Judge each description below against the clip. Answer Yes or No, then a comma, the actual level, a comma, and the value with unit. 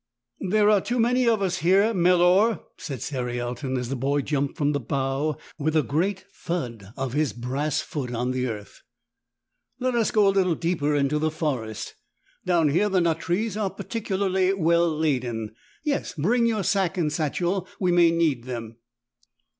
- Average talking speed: Yes, average, 175 wpm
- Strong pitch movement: Yes, wide, 6.1 semitones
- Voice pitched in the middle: Yes, medium, 160 Hz